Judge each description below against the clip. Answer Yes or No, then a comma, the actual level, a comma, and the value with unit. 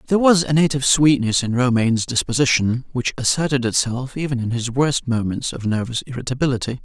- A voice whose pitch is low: Yes, low, 130 Hz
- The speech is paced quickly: No, average, 165 wpm